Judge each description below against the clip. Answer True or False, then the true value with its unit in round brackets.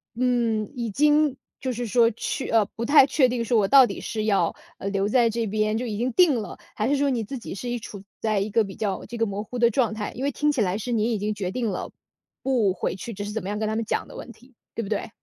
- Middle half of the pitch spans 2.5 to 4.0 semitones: True (3.1 semitones)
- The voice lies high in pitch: True (225 Hz)